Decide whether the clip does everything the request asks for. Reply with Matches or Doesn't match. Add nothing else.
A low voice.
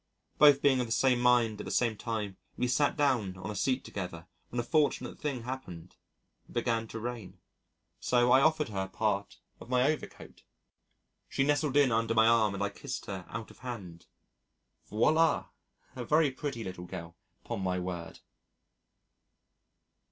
Matches